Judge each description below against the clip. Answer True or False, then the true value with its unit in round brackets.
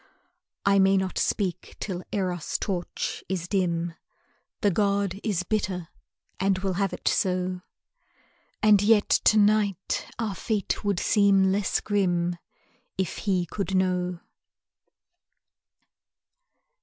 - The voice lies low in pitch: False (190 Hz)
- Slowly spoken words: True (115 wpm)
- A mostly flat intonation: True (2.1 semitones)